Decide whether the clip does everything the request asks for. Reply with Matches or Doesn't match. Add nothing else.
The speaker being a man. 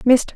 Doesn't match